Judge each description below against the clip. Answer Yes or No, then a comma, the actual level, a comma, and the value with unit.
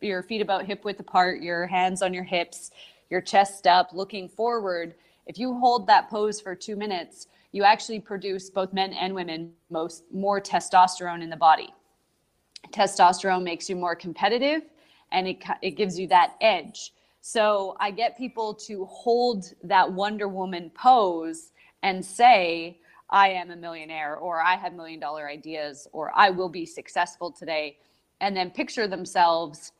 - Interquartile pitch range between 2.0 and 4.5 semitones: Yes, average, 3.4 semitones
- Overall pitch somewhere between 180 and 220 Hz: Yes, medium, 185 Hz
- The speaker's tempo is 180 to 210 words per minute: No, average, 165 wpm